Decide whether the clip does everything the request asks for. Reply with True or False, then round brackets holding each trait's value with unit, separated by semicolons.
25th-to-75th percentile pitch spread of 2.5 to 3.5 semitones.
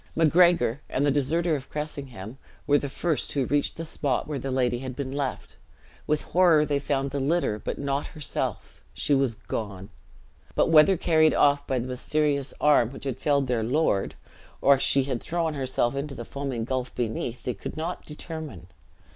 True (3.0 semitones)